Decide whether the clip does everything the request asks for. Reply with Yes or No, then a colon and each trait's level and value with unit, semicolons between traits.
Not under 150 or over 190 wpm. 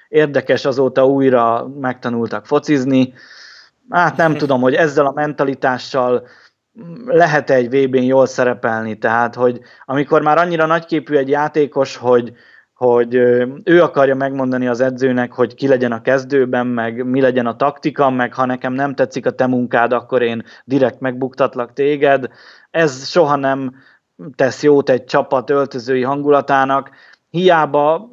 No: average, 140 wpm